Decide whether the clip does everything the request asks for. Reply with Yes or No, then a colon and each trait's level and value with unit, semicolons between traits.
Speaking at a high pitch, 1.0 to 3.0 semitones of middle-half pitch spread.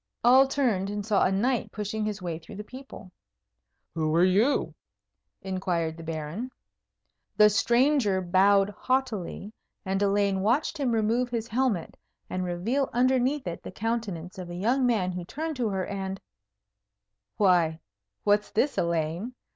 No: high, 205 Hz; average, 4.9 semitones